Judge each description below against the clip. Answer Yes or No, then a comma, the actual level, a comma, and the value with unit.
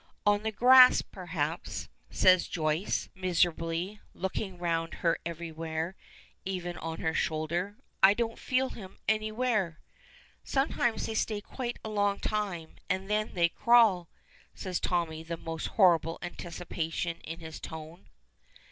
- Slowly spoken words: Yes, slow, 130 wpm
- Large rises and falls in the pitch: No, average, 4.2 semitones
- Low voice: No, medium, 180 Hz